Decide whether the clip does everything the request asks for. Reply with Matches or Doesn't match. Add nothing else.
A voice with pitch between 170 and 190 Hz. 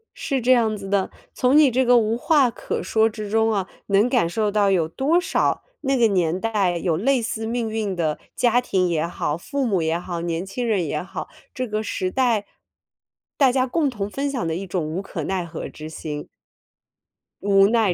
Doesn't match